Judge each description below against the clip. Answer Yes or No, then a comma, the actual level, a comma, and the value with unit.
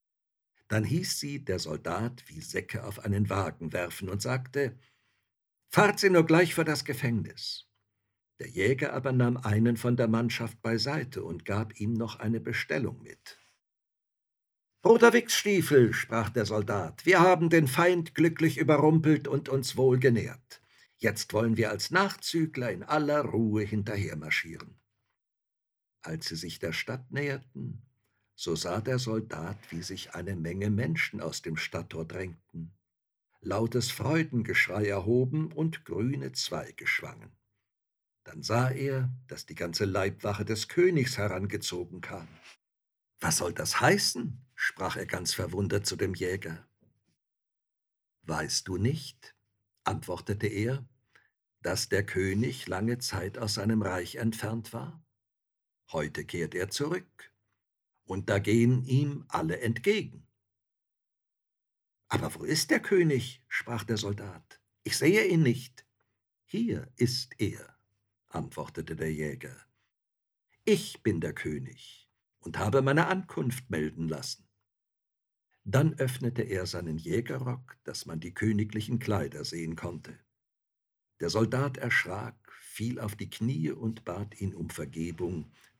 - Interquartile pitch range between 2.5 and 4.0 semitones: No, average, 4.6 semitones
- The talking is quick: No, average, 130 wpm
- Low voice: Yes, low, 115 Hz